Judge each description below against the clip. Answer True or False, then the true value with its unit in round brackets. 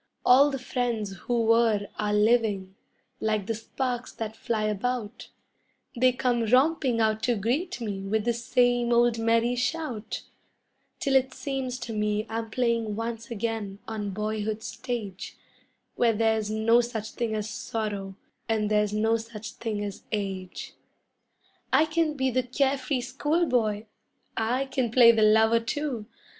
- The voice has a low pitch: False (230 Hz)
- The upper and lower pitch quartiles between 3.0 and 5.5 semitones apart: False (2.6 semitones)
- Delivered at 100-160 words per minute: True (150 wpm)